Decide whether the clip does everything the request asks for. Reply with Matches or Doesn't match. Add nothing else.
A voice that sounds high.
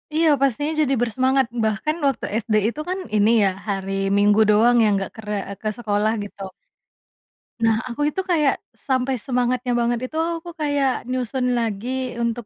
Matches